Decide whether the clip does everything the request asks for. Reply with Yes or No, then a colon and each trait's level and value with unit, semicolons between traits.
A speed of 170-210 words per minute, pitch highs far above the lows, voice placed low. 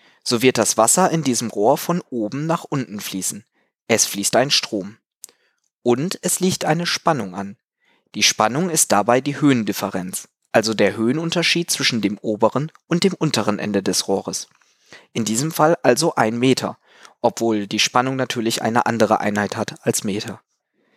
No: average, 160 wpm; wide, 6.5 semitones; low, 120 Hz